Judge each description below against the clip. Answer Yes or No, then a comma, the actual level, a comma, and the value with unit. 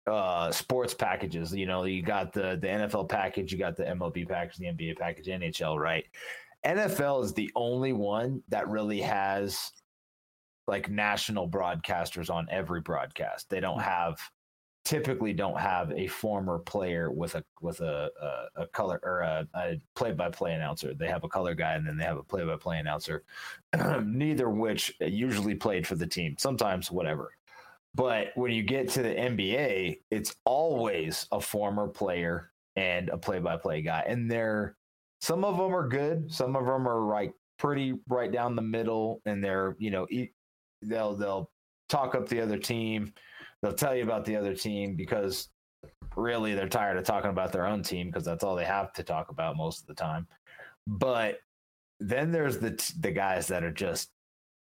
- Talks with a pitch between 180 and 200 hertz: No, low, 105 Hz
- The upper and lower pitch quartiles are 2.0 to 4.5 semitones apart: No, average, 4.9 semitones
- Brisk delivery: No, average, 180 wpm